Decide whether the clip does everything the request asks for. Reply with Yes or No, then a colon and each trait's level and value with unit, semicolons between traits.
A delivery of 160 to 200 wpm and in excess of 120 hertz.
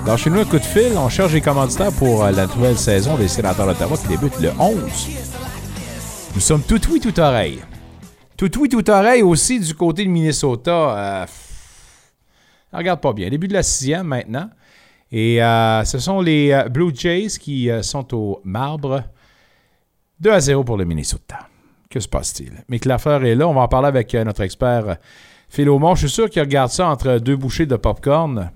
Yes: average, 195 wpm; low, 135 Hz